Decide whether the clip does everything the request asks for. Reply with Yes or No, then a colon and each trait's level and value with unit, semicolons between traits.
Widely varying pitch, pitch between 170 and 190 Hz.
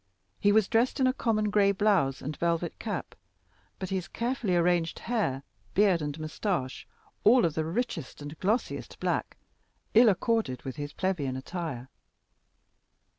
Yes: wide, 6.0 semitones; medium, 185 Hz